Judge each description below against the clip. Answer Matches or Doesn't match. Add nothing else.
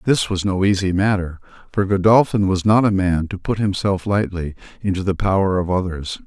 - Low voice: Matches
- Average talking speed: Matches